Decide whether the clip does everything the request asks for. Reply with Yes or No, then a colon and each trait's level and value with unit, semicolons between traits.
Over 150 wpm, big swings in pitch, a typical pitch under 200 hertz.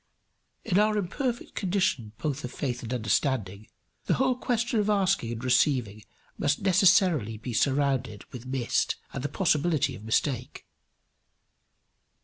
No: slow, 135 wpm; wide, 8.2 semitones; medium, 140 Hz